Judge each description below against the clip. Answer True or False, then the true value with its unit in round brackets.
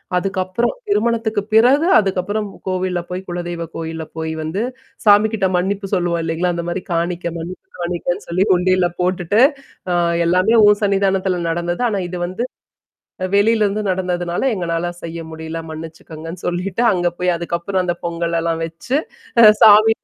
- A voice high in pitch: False (180 Hz)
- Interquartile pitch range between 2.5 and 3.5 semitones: True (2.8 semitones)